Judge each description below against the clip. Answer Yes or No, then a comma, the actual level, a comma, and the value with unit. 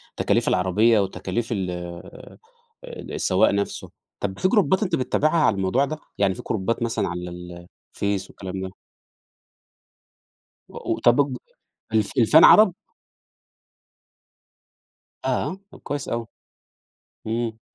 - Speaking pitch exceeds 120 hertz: No, low, 110 Hz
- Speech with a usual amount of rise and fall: No, wide, 6.6 semitones